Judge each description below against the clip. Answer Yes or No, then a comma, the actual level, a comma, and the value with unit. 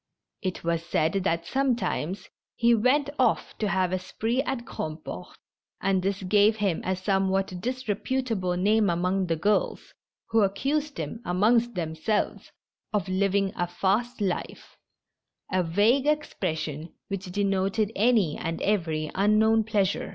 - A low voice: No, high, 195 Hz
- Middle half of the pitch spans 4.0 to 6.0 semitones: No, average, 3.6 semitones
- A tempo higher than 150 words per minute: No, slow, 135 wpm